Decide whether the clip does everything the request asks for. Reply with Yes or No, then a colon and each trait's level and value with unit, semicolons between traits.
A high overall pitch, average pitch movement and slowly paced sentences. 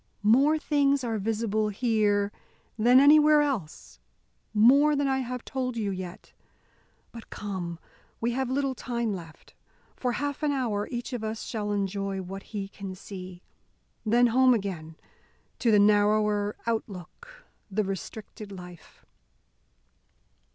Yes: high, 220 Hz; average, 4.3 semitones; slow, 130 wpm